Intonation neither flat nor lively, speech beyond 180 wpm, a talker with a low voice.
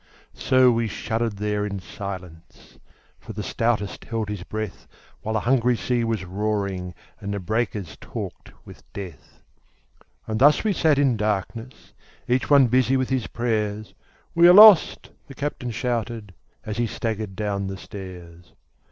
No: average, 3.5 semitones; average, 150 wpm; low, 110 Hz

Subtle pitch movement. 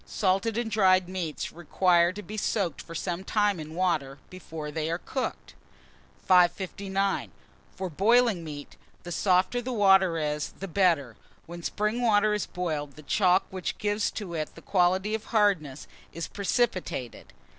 No: average, 3.9 semitones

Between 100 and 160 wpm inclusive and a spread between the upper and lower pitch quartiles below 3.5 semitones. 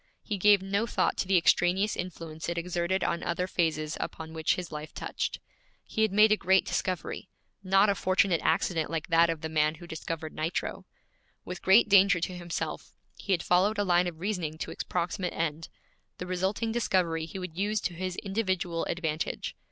No: average, 190 wpm; average, 2.8 semitones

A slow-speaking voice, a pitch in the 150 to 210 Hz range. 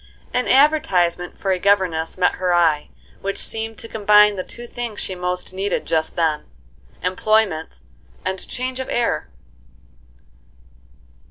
Yes: slow, 125 wpm; high, 190 Hz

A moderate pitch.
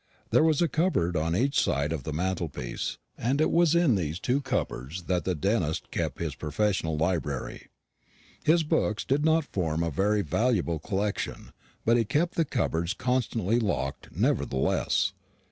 No: low, 100 Hz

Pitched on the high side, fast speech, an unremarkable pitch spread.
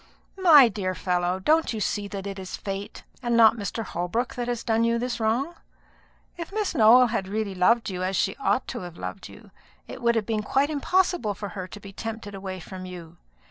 Yes: high, 215 Hz; fast, 215 wpm; average, 3.9 semitones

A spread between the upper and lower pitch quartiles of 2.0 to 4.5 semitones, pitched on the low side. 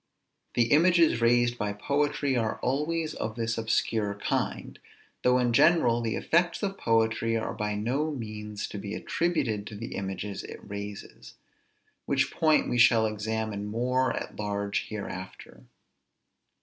Yes: average, 4.0 semitones; low, 115 Hz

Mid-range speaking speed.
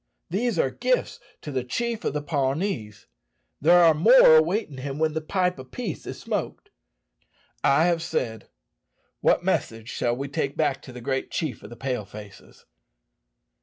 Yes: average, 165 wpm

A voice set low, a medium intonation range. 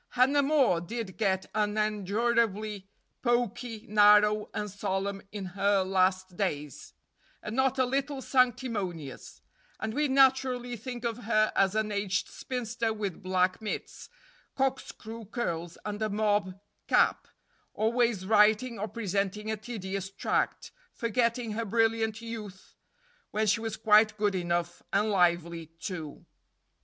No: high, 215 Hz; average, 3.3 semitones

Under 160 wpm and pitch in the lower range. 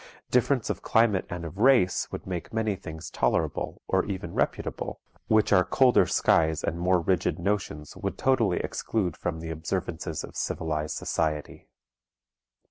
Yes: average, 145 wpm; very low, 90 Hz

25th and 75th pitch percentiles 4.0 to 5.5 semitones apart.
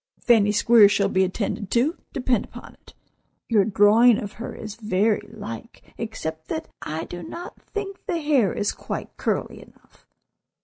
No: average, 3.3 semitones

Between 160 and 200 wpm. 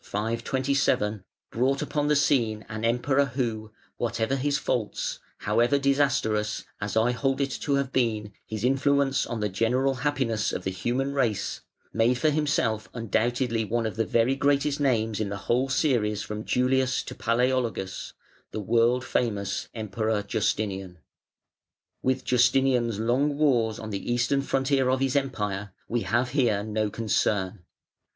No: average, 145 wpm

